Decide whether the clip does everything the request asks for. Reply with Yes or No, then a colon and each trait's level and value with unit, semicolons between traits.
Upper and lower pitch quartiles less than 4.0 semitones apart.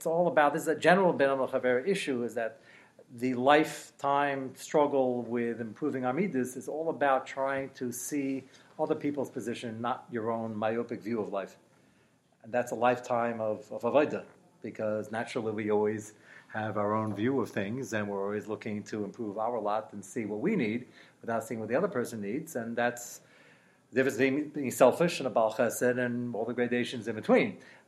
Yes: average, 3.4 semitones